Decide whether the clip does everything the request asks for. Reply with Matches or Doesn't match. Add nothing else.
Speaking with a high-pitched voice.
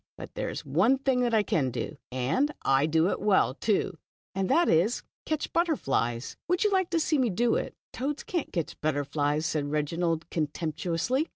Doesn't match